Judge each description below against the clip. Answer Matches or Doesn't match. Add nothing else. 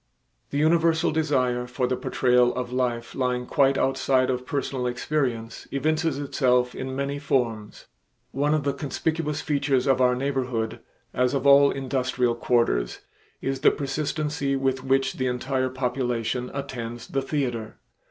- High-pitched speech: Doesn't match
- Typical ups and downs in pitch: Doesn't match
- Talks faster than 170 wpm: Doesn't match